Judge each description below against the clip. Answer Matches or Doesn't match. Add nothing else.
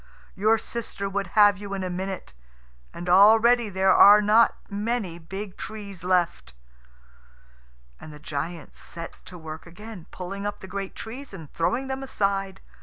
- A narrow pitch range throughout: Doesn't match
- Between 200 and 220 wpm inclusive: Doesn't match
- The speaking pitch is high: Matches